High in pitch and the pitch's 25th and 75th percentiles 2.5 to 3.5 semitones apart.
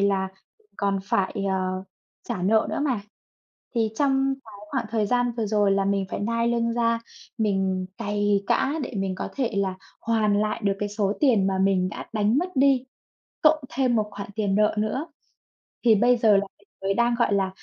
Yes: high, 210 Hz; average, 3.2 semitones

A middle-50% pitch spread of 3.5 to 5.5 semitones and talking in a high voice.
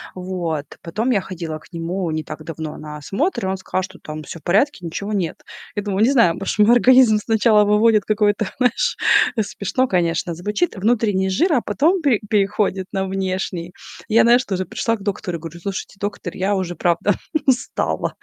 Yes: average, 3.9 semitones; high, 195 Hz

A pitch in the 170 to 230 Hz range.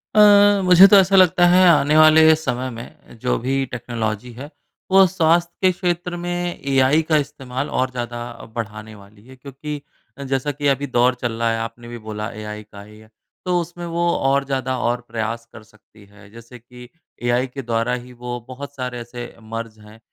No: low, 125 Hz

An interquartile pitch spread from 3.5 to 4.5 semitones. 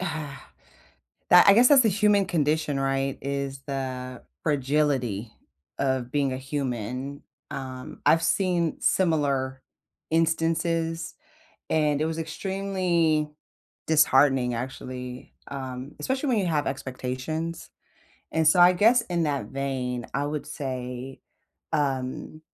Yes: average, 3.8 semitones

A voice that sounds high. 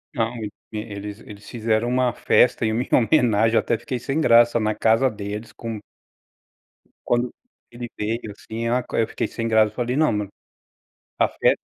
No: low, 115 Hz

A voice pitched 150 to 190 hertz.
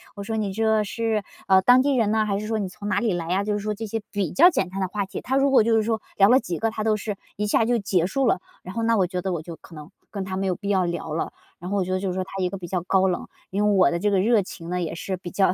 No: high, 200 Hz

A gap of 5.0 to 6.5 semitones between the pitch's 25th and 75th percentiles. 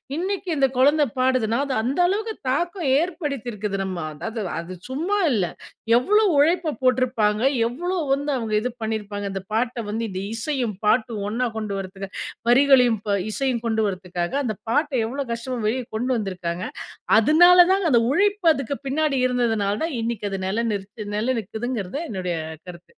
Yes: wide, 5.4 semitones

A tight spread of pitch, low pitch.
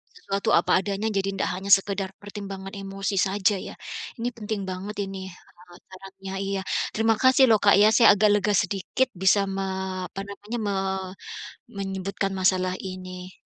No: narrow, 1.3 semitones; high, 195 Hz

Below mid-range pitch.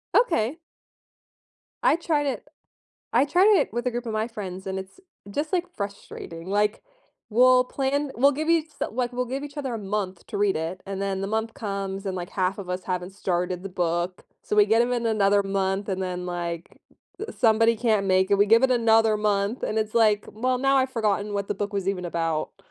No: high, 210 Hz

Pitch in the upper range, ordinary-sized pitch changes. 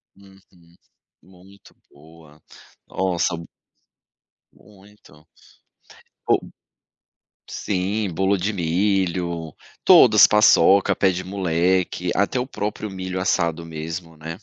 No: very low, 90 Hz; average, 3.0 semitones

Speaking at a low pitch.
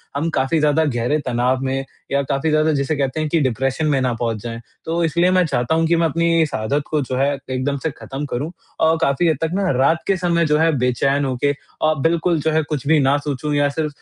No: medium, 150 Hz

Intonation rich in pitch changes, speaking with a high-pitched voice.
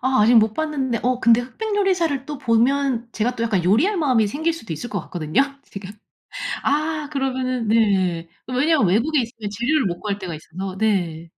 Yes: wide, 5.7 semitones; high, 235 Hz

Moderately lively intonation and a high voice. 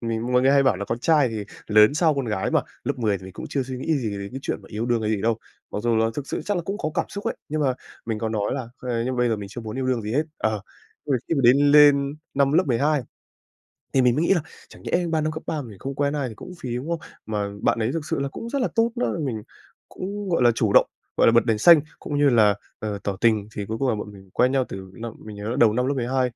No: average, 4.8 semitones; low, 125 Hz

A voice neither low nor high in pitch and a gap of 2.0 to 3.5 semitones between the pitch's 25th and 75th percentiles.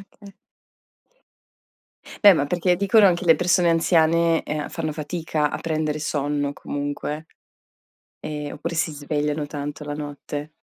Yes: medium, 155 Hz; narrow, 2.4 semitones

